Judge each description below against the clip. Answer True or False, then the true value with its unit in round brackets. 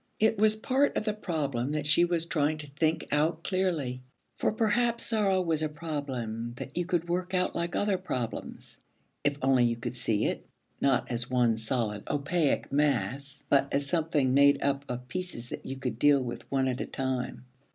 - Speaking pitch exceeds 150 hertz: False (145 Hz)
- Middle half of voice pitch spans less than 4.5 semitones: False (5.3 semitones)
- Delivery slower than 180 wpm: False (190 wpm)